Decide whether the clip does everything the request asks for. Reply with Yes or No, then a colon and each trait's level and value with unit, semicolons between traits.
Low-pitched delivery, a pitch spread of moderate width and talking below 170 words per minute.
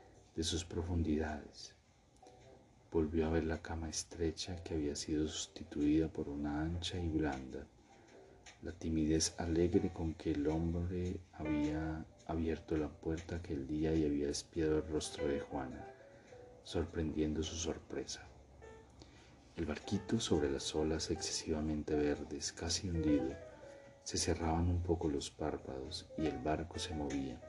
No: very low, 80 Hz; narrow, 1.7 semitones; average, 135 wpm